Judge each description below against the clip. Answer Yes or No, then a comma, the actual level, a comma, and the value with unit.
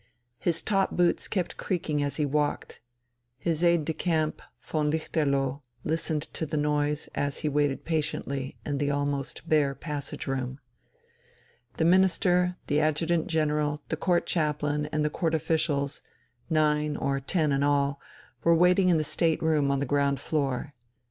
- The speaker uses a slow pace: No, average, 155 wpm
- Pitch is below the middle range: No, medium, 150 Hz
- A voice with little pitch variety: Yes, narrow, 2.2 semitones